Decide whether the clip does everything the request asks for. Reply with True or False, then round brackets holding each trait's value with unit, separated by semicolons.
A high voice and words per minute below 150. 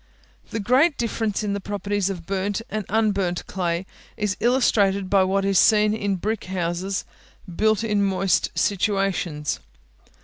True (200 Hz; 140 wpm)